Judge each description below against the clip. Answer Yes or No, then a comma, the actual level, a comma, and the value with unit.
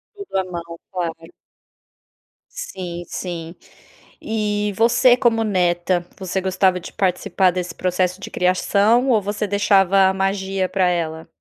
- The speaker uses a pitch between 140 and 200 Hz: Yes, high, 190 Hz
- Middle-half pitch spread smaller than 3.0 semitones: Yes, narrow, 2.5 semitones